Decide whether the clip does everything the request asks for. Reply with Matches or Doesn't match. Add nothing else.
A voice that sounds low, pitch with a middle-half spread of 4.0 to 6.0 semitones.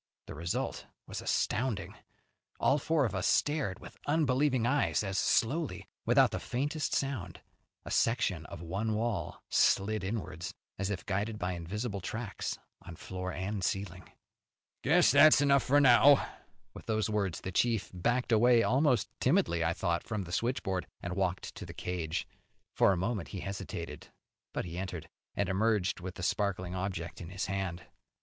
Matches